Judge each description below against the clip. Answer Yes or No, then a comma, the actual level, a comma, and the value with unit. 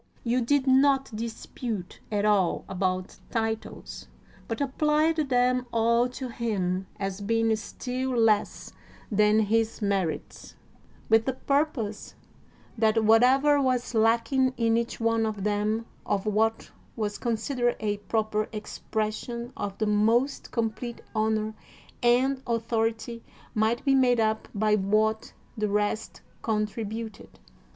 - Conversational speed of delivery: No, slow, 120 wpm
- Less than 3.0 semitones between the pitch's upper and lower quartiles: Yes, narrow, 2.5 semitones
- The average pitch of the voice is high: Yes, high, 225 Hz